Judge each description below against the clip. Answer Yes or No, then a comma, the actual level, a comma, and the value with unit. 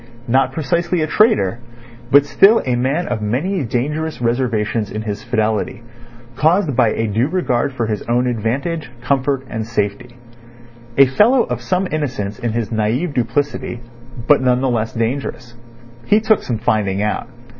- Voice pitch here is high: No, low, 125 Hz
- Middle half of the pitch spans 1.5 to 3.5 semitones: No, average, 4.8 semitones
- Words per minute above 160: No, average, 155 wpm